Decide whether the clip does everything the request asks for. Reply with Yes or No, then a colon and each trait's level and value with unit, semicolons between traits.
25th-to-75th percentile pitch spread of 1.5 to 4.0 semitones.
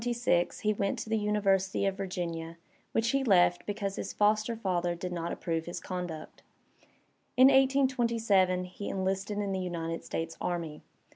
Yes: average, 3.6 semitones